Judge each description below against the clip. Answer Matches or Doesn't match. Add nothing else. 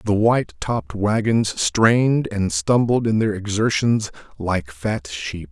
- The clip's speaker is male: Matches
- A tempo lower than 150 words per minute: Matches